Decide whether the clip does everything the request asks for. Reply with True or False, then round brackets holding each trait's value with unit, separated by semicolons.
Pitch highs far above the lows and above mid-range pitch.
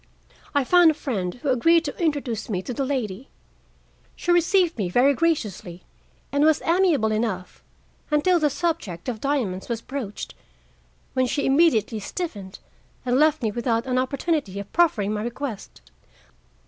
True (6.3 semitones; 255 Hz)